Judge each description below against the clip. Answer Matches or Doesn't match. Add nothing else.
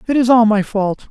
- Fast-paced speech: Matches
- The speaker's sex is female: Doesn't match